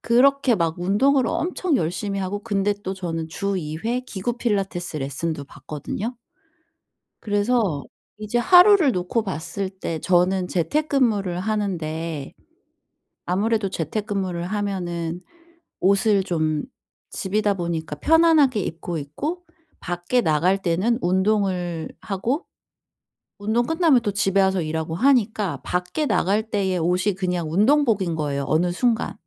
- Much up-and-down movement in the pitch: No, average, 4.7 semitones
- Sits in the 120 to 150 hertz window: No, high, 195 Hz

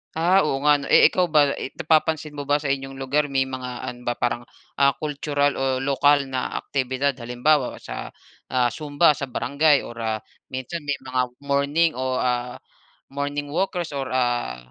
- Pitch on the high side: No, medium, 140 Hz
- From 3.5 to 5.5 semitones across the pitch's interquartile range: No, narrow, 2.4 semitones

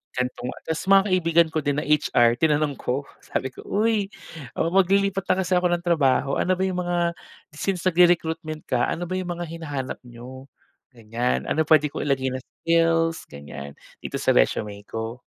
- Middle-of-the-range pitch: Yes, medium, 155 Hz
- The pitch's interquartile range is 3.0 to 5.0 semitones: No, wide, 5.5 semitones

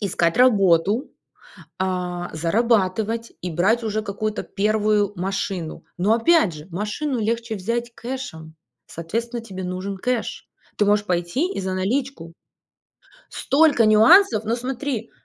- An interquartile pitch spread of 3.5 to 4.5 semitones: Yes, average, 4.2 semitones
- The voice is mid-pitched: No, high, 210 Hz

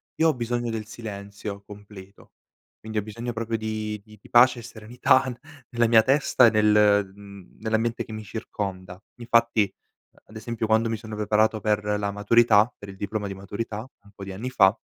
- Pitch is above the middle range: No, low, 110 Hz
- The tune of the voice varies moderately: No, narrow, 2.2 semitones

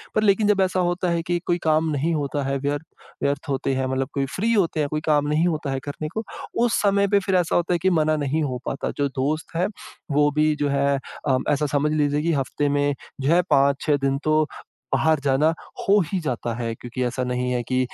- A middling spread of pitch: Yes, average, 3.4 semitones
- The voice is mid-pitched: Yes, medium, 150 Hz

